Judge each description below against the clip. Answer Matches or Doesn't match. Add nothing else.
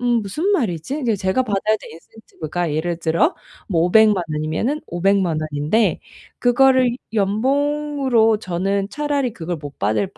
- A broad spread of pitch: Matches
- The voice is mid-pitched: Doesn't match